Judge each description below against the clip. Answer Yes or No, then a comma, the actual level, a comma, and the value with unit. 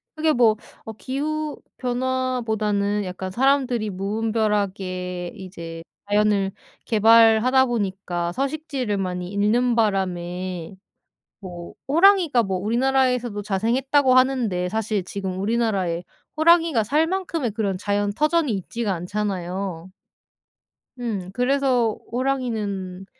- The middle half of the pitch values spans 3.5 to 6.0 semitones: Yes, average, 5.1 semitones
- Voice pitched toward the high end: Yes, high, 215 Hz